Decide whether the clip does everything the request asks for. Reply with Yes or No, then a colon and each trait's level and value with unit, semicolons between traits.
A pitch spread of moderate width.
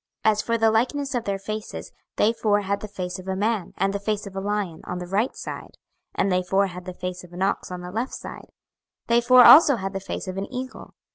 Yes: average, 3.1 semitones